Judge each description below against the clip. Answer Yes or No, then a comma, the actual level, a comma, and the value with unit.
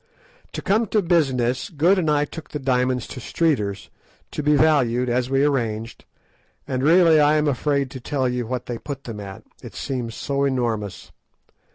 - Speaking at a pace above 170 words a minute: Yes, average, 180 wpm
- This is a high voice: No, low, 135 Hz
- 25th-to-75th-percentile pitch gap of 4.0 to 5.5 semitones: No, average, 3.5 semitones